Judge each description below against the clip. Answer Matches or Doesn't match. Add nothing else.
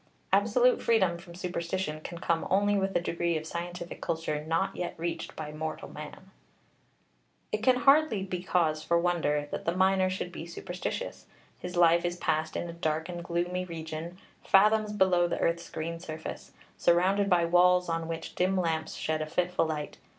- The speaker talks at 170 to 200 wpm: Matches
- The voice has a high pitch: Doesn't match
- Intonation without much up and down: Matches